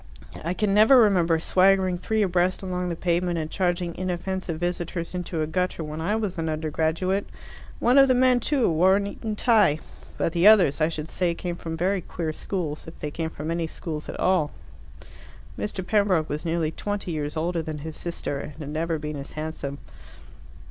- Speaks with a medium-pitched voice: Yes, medium, 175 Hz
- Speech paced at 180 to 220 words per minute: Yes, average, 190 wpm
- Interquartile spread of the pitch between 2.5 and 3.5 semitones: Yes, average, 3.2 semitones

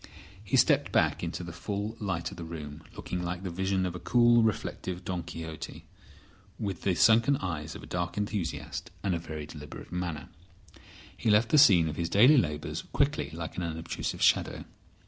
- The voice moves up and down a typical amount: Yes, average, 3.8 semitones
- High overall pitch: No, very low, 90 Hz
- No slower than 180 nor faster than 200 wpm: Yes, average, 185 wpm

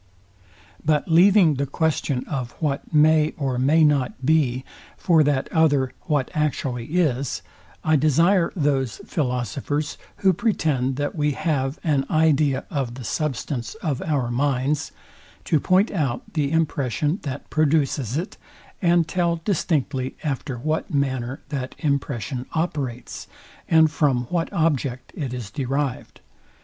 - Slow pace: Yes, slow, 130 wpm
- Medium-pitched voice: Yes, medium, 145 Hz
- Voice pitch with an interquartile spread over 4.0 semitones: No, average, 3.4 semitones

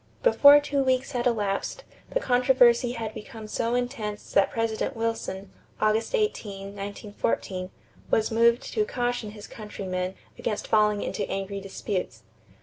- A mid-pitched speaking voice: No, high, 220 Hz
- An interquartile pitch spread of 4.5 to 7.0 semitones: No, average, 3.3 semitones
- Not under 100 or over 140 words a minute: Yes, slow, 135 wpm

